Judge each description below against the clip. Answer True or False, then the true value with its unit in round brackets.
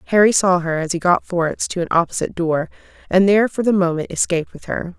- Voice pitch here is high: False (180 Hz)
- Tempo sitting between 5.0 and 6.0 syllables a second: False (6.7 syllables/s)